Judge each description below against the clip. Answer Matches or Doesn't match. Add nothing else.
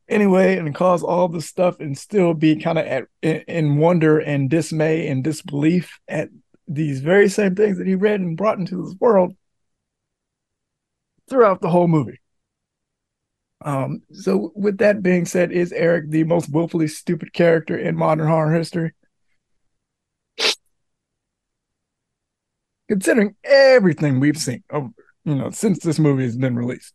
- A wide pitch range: Doesn't match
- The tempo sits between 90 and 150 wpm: Matches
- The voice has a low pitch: Doesn't match